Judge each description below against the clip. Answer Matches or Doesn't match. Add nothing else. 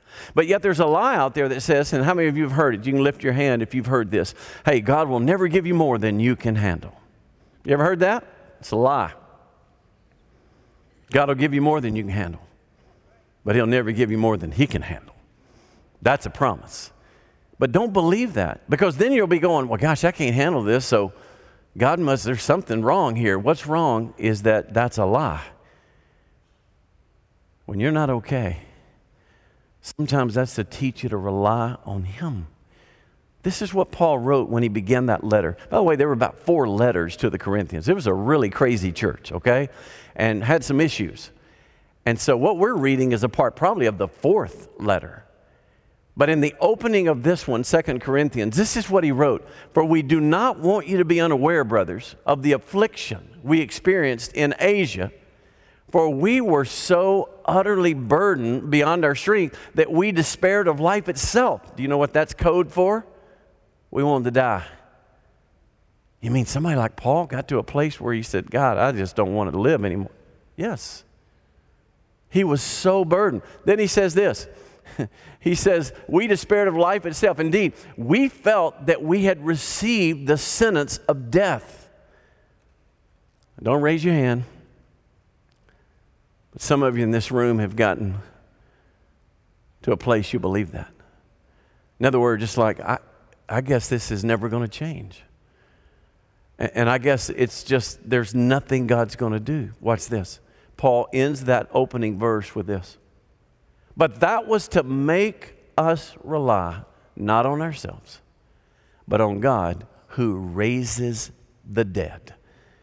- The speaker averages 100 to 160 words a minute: Doesn't match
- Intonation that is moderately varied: Doesn't match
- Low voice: Matches